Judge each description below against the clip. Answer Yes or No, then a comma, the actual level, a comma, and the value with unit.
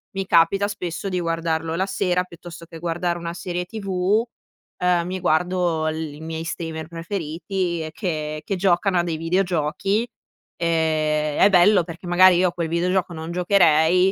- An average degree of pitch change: No, narrow, 2.2 semitones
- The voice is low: No, medium, 175 Hz